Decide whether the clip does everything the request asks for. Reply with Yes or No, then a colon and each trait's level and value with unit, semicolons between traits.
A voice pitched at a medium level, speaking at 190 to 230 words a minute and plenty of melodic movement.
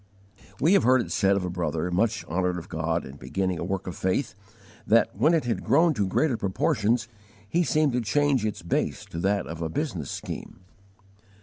No: low, 100 Hz; average, 200 wpm; wide, 6.2 semitones